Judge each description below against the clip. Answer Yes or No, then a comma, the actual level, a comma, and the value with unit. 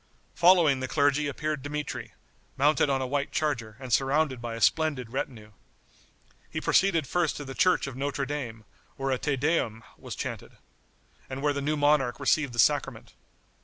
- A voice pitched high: No, medium, 140 Hz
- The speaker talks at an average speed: Yes, average, 170 wpm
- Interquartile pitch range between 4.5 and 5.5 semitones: No, narrow, 2.6 semitones